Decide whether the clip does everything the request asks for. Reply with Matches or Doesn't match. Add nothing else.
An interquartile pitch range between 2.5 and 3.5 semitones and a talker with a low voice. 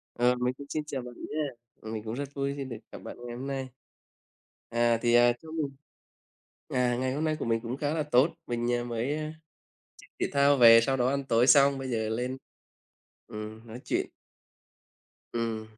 Matches